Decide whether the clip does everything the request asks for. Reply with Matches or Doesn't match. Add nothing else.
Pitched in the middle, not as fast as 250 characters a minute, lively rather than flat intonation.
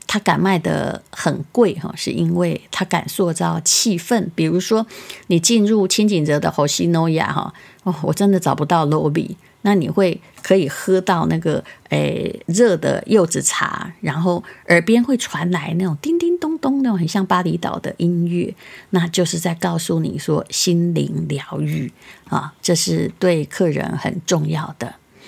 Doesn't match